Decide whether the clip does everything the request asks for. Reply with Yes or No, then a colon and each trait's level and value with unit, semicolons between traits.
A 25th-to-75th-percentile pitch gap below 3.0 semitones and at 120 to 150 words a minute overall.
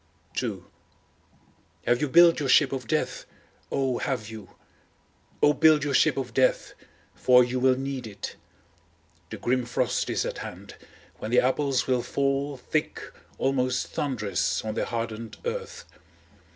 Yes: narrow, 2.4 semitones; average, 145 wpm